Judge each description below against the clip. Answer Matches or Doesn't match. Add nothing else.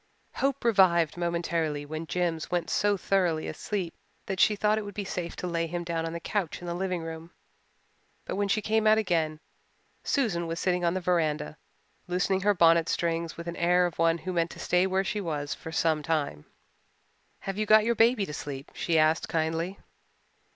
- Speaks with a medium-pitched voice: Matches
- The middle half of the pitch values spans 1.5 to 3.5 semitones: Matches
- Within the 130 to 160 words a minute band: Doesn't match